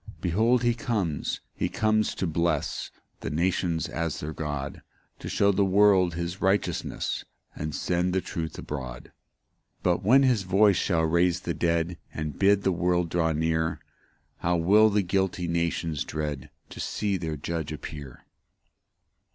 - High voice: No, very low, 85 Hz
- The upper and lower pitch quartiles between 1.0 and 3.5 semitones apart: Yes, average, 3.2 semitones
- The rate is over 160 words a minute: No, average, 155 wpm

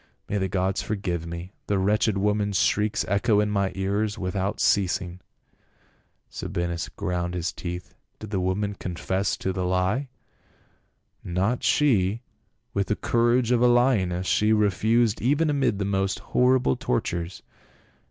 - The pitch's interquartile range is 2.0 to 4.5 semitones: Yes, average, 2.9 semitones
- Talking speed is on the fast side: No, average, 150 wpm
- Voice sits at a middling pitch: No, low, 100 Hz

